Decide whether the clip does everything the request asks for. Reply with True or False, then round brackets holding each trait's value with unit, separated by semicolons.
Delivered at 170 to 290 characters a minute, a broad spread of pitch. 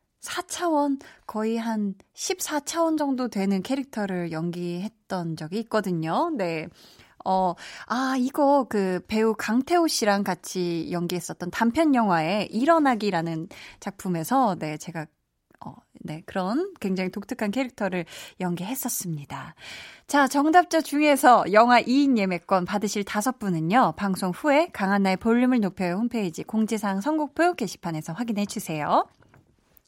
True (285 characters per minute; 6.6 semitones)